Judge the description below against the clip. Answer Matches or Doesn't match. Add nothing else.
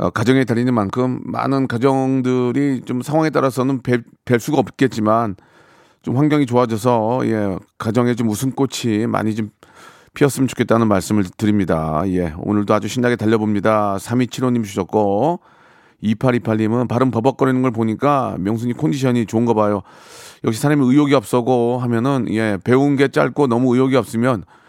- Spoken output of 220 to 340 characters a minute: Matches